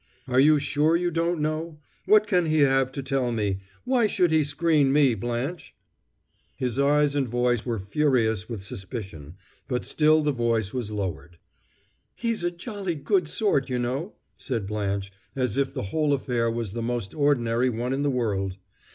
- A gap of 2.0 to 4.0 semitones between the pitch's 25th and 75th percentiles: No, average, 5.1 semitones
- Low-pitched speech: Yes, low, 130 Hz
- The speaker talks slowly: No, average, 175 wpm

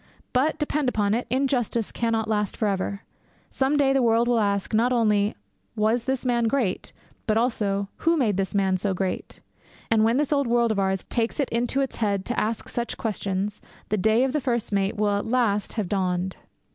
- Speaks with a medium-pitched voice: No, high, 225 Hz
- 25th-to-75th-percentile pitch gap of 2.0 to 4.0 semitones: Yes, average, 3.5 semitones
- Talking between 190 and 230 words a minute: Yes, average, 200 wpm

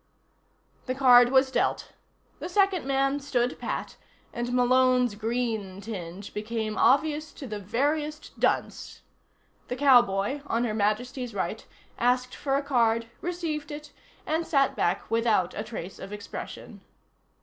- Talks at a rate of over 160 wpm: No, slow, 135 wpm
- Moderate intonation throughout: Yes, average, 4.3 semitones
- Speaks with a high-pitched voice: Yes, high, 245 Hz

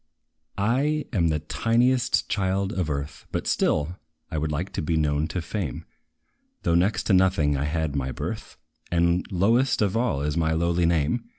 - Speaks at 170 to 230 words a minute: Yes, average, 175 wpm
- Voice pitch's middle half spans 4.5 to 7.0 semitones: Yes, average, 5.0 semitones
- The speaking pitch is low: Yes, very low, 85 Hz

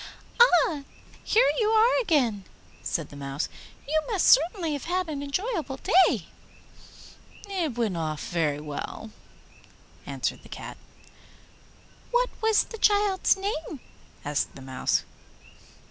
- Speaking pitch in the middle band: No, very high, 315 Hz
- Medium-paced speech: No, slow, 120 wpm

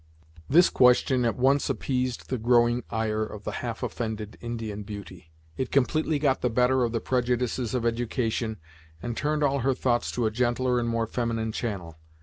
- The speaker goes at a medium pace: Yes, average, 175 wpm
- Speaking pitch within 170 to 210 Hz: No, low, 120 Hz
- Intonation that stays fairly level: Yes, narrow, 2.3 semitones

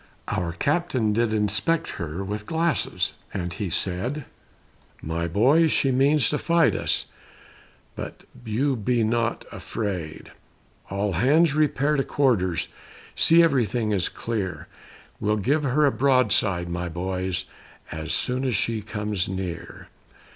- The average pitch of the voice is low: Yes, low, 110 Hz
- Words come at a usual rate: No, slow, 130 wpm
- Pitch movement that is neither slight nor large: No, wide, 6.6 semitones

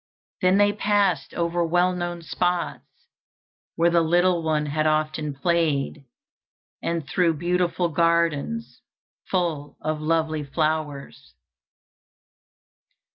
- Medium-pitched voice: Yes, medium, 170 Hz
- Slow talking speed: Yes, slow, 100 wpm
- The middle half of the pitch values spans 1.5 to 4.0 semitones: Yes, narrow, 2.4 semitones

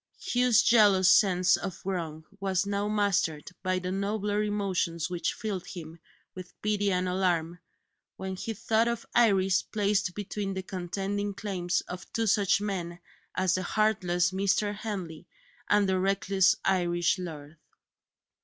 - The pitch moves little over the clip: Yes, narrow, 2.3 semitones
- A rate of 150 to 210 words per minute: No, average, 140 wpm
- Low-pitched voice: No, high, 190 Hz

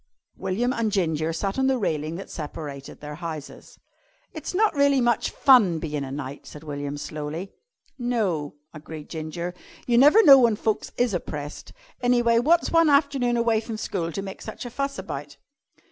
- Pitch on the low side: No, high, 195 Hz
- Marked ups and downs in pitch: Yes, wide, 7.9 semitones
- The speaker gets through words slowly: No, average, 175 wpm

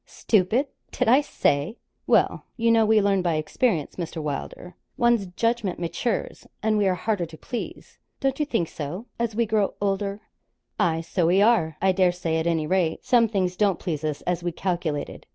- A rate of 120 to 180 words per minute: No, average, 190 wpm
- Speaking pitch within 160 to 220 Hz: Yes, high, 190 Hz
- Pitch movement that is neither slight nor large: Yes, average, 4.9 semitones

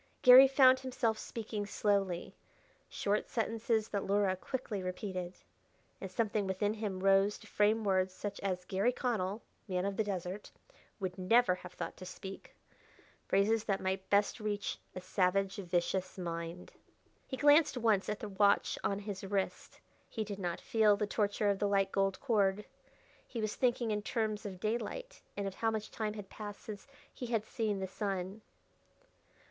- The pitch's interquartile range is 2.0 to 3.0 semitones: Yes, narrow, 2.4 semitones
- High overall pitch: Yes, high, 205 Hz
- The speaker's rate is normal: Yes, average, 165 wpm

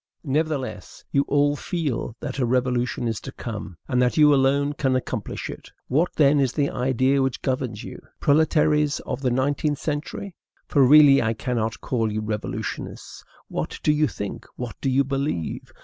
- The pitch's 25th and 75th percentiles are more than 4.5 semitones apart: No, average, 2.9 semitones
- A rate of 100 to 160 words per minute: No, average, 170 wpm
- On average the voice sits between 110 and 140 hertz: Yes, low, 135 Hz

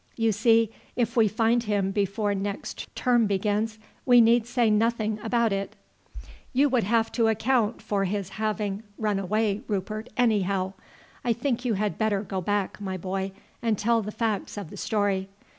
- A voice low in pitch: No, high, 215 Hz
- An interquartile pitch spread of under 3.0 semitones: Yes, narrow, 2.4 semitones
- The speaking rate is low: No, average, 170 wpm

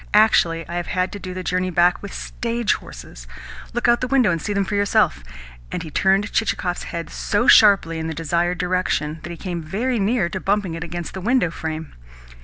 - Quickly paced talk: Yes, fast, 215 wpm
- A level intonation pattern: No, average, 3.4 semitones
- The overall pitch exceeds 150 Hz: Yes, medium, 185 Hz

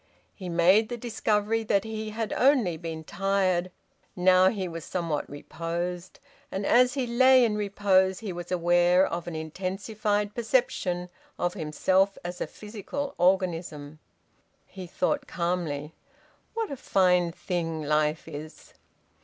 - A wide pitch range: No, average, 3.8 semitones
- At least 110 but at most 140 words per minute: Yes, slow, 135 wpm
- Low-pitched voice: No, medium, 185 Hz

